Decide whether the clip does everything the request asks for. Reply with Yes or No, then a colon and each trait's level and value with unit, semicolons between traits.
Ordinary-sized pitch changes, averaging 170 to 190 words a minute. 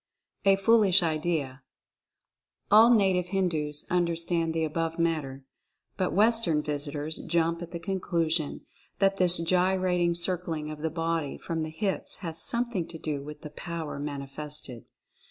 No: average, 3.0 semitones; average, 140 wpm